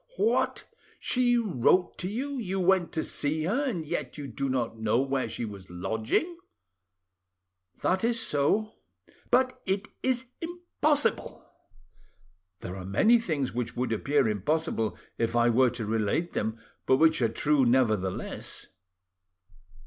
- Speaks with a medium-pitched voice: Yes, medium, 145 Hz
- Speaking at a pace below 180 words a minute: Yes, average, 140 wpm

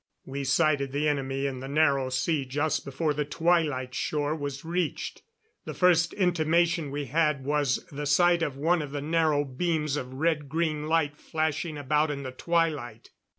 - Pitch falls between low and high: Yes, medium, 150 Hz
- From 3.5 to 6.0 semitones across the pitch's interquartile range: No, average, 2.8 semitones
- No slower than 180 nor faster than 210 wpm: No, average, 170 wpm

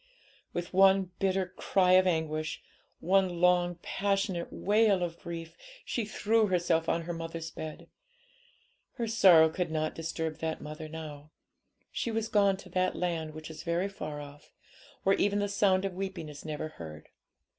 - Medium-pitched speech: Yes, medium, 175 Hz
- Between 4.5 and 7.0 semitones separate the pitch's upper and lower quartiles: No, average, 3.4 semitones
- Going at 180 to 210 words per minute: No, average, 160 wpm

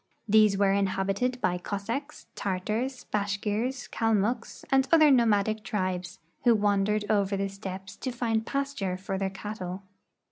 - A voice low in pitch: No, high, 205 Hz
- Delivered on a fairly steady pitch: No, average, 3.2 semitones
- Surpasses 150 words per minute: No, average, 145 wpm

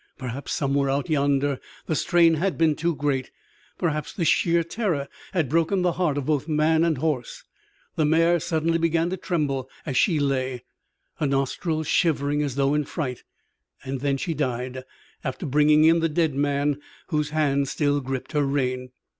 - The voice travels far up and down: No, average, 2.9 semitones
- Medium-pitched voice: Yes, medium, 150 Hz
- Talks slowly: No, average, 170 wpm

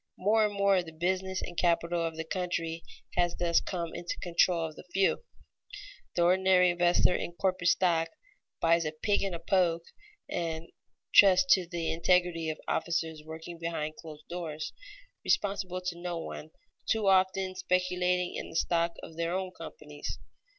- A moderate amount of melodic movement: No, narrow, 1.9 semitones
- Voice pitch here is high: No, medium, 175 Hz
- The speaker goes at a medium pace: Yes, average, 165 wpm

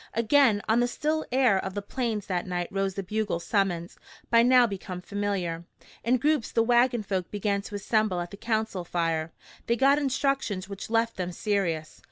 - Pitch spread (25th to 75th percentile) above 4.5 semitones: No, average, 4.2 semitones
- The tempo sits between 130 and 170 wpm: No, average, 185 wpm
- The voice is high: Yes, high, 205 Hz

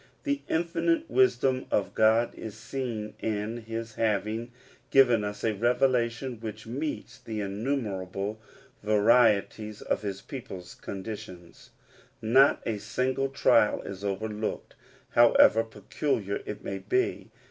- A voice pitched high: No, low, 110 Hz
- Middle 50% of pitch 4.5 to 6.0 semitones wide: No, average, 3.5 semitones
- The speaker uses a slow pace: Yes, slow, 115 wpm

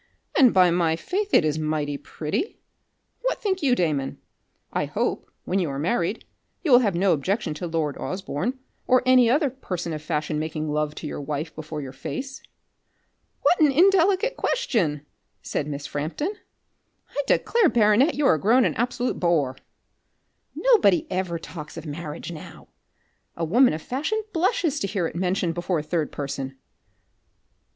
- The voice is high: No, medium, 180 Hz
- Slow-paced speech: No, average, 160 wpm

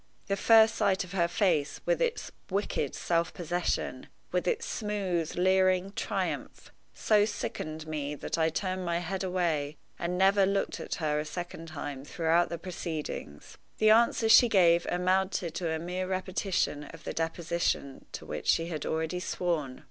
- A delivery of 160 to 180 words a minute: Yes, average, 165 wpm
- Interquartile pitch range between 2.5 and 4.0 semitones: Yes, average, 3.0 semitones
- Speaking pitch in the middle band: Yes, medium, 175 Hz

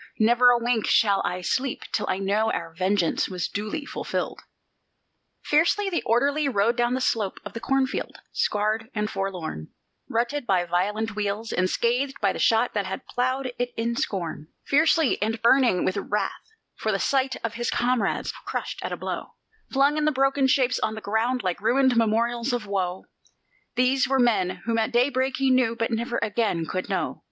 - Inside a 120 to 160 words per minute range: No, average, 180 wpm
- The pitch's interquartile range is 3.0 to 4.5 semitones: Yes, average, 4.0 semitones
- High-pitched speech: Yes, high, 230 Hz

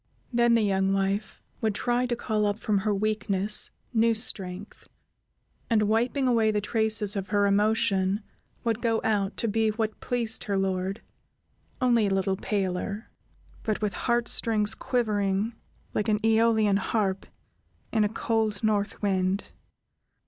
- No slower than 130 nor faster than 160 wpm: Yes, average, 145 wpm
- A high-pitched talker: Yes, high, 215 Hz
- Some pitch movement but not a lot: No, narrow, 2.1 semitones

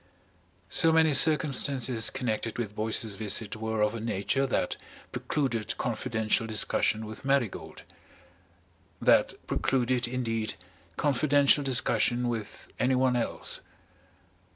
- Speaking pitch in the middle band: No, low, 120 Hz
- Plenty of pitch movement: No, average, 3.3 semitones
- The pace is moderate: No, slow, 105 wpm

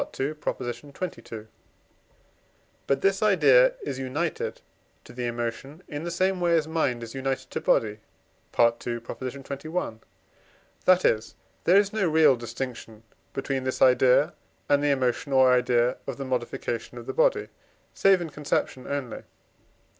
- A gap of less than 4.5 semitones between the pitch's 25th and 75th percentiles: No, average, 5.0 semitones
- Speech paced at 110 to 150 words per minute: Yes, average, 140 wpm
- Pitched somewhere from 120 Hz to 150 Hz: Yes, low, 135 Hz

